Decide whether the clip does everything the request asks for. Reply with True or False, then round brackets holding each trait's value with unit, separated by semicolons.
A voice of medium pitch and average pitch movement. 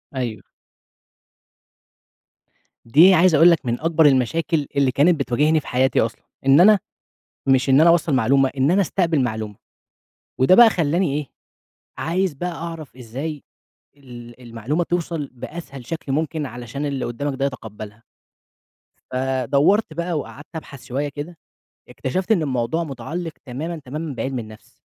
True (145 Hz; 4.4 semitones)